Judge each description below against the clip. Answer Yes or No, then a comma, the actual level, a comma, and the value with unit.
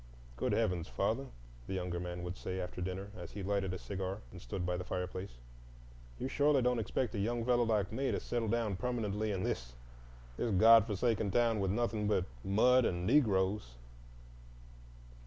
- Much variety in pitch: No, average, 4.1 semitones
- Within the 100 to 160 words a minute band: No, average, 175 wpm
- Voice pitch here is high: No, low, 100 Hz